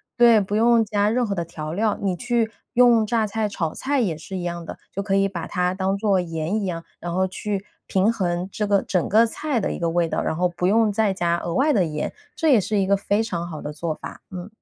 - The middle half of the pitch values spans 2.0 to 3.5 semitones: No, average, 4.0 semitones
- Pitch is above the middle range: Yes, high, 195 Hz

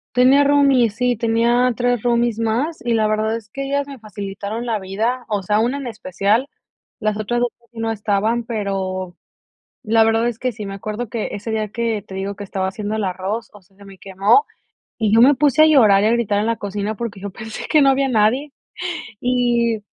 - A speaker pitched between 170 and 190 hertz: No, high, 225 Hz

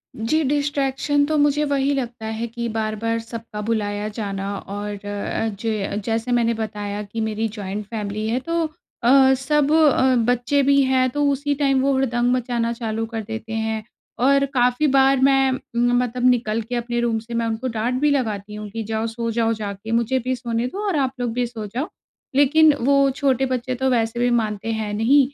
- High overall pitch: Yes, high, 235 Hz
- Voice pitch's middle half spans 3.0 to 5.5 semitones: Yes, average, 3.3 semitones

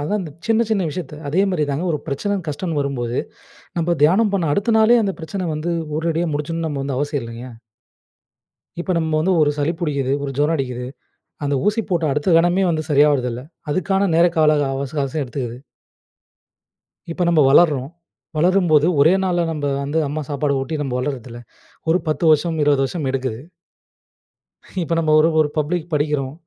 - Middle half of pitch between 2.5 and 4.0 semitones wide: Yes, average, 3.7 semitones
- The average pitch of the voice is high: No, medium, 155 Hz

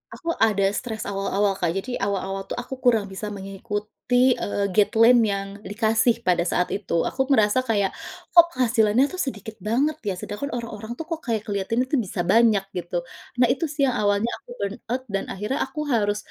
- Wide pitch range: No, average, 3.8 semitones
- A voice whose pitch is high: Yes, high, 215 Hz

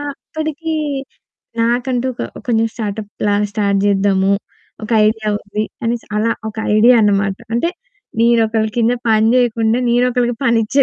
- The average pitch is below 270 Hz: Yes, high, 230 Hz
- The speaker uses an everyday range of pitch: No, narrow, 2.3 semitones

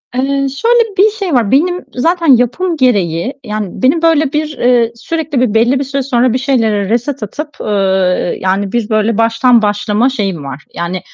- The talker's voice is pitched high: Yes, high, 245 Hz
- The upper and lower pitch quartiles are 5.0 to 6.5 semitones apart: Yes, average, 5.3 semitones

